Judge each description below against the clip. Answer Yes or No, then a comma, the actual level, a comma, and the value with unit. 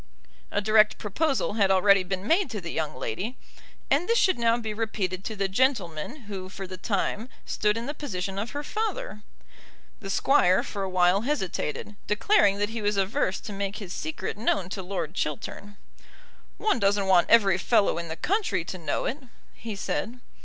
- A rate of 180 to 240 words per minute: Yes, average, 185 wpm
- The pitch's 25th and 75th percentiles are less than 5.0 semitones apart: Yes, average, 3.7 semitones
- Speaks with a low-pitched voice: No, high, 205 Hz